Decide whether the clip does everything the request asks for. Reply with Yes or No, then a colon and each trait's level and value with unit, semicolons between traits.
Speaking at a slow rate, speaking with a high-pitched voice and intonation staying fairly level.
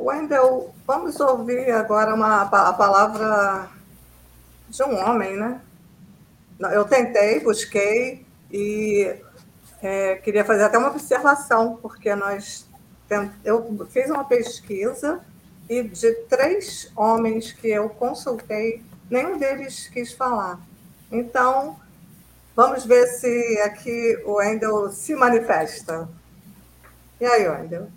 No: slow, 105 wpm; high, 220 Hz; average, 3.7 semitones